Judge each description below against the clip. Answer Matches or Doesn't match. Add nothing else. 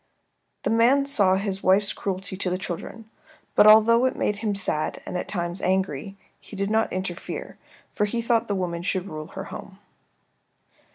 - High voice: Matches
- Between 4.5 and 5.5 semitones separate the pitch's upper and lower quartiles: Doesn't match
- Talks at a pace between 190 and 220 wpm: Doesn't match